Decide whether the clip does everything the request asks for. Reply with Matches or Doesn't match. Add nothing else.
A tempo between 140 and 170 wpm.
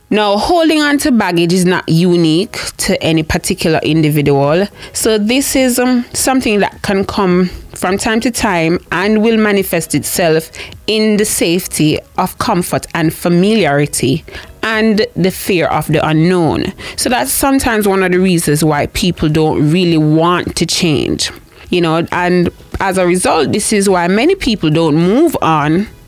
Matches